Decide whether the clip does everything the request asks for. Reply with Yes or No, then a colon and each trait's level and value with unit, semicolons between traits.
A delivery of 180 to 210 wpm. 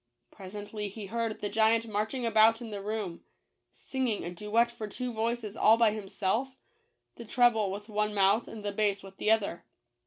Yes: average, 190 wpm